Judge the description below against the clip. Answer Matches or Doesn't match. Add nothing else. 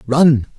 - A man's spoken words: Matches